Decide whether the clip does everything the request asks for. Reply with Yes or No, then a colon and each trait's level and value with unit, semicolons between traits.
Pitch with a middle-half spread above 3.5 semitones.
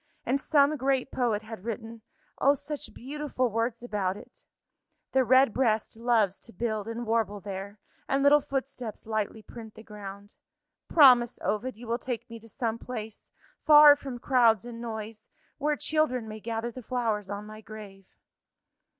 No: average, 3.1 semitones